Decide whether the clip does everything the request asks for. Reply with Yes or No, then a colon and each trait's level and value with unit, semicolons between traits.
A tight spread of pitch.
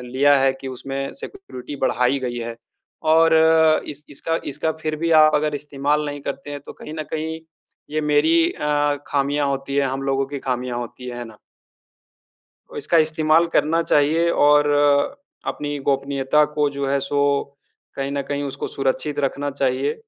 Yes: narrow, 1.8 semitones